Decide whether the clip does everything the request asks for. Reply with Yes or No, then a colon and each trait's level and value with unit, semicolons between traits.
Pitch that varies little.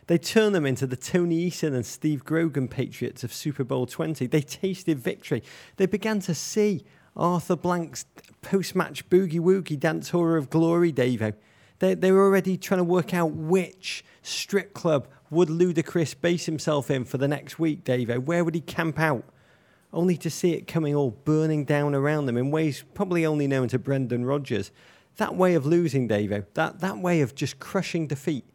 No: average, 4.2 semitones